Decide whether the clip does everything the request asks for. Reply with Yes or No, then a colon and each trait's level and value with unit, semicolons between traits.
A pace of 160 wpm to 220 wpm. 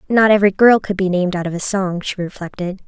No: fast, 250 wpm